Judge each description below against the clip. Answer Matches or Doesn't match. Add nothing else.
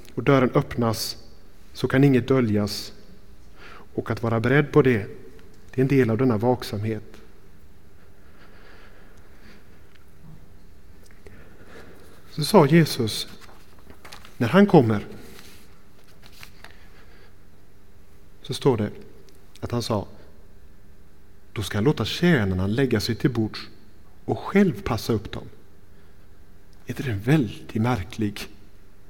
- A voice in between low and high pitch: Doesn't match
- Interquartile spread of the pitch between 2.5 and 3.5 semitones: Matches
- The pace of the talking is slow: Matches